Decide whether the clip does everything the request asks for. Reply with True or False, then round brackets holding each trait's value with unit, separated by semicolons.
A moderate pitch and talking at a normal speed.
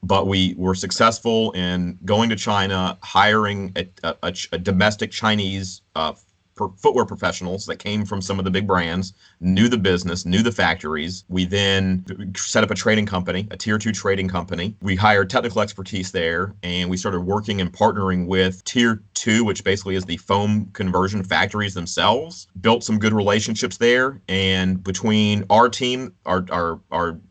False (95 Hz; 175 wpm)